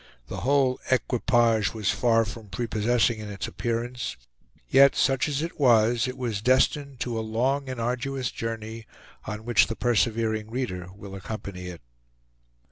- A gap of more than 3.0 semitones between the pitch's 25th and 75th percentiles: No, average, 2.7 semitones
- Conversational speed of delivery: Yes, average, 150 wpm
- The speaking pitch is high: No, low, 115 Hz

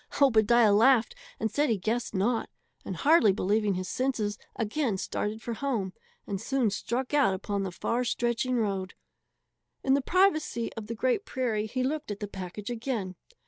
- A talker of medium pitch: No, high, 225 Hz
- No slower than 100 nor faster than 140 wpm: No, average, 170 wpm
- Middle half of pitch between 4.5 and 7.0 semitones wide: No, average, 4.0 semitones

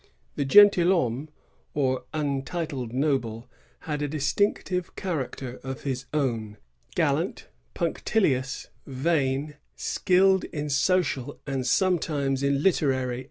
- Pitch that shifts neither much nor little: Yes, average, 4.0 semitones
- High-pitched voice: No, medium, 140 Hz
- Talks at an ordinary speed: No, slow, 105 wpm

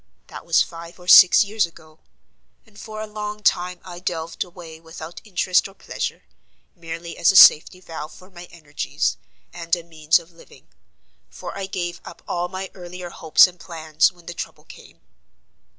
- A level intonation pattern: Yes, narrow, 2.0 semitones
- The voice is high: No, medium, 175 Hz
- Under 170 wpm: No, average, 175 wpm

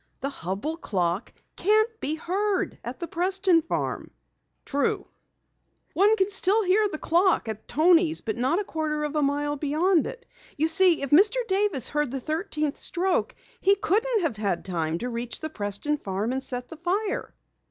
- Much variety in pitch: Yes, wide, 6.4 semitones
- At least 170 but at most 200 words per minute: Yes, average, 175 wpm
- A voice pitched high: Yes, very high, 315 Hz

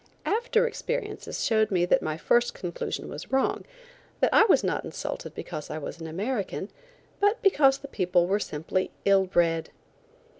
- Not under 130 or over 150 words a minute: No, average, 160 wpm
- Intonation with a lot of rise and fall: Yes, wide, 8.2 semitones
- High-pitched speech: Yes, high, 200 Hz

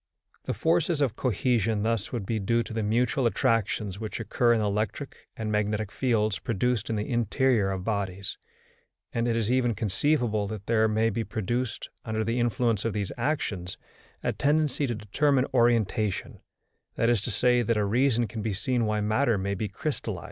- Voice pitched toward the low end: Yes, low, 115 Hz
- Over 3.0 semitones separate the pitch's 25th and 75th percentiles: No, narrow, 2.6 semitones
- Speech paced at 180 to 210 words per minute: Yes, average, 185 wpm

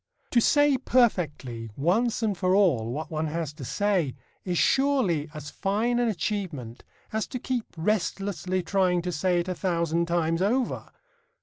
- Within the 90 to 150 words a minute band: No, average, 160 wpm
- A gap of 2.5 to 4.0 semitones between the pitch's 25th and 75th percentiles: No, average, 5.1 semitones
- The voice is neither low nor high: Yes, medium, 180 Hz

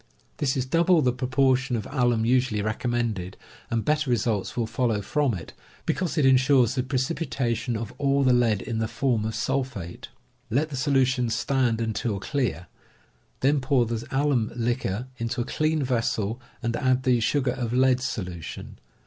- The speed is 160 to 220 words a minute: Yes, average, 165 wpm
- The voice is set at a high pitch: No, low, 125 Hz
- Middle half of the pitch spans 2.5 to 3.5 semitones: Yes, average, 2.8 semitones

